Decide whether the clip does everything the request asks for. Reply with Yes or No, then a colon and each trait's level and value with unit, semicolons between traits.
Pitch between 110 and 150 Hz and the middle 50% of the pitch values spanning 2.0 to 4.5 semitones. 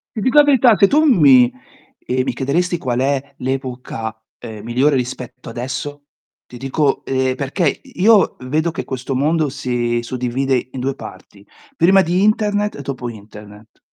No: low, 135 Hz; wide, 5.4 semitones